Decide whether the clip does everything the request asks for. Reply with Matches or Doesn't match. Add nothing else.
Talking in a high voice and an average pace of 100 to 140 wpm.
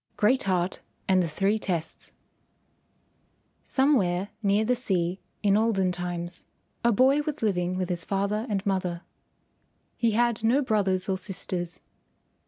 Matches